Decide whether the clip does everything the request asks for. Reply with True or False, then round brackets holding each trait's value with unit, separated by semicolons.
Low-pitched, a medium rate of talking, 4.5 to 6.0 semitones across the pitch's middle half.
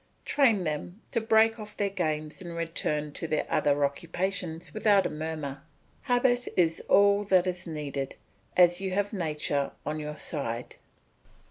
False (170 Hz; 150 wpm; 5.0 semitones)